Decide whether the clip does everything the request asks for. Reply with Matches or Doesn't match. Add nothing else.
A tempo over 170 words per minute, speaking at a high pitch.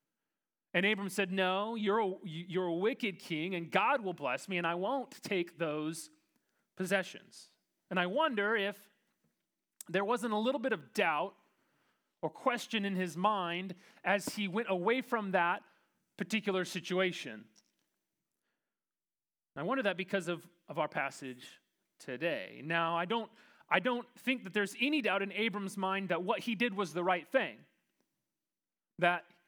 Doesn't match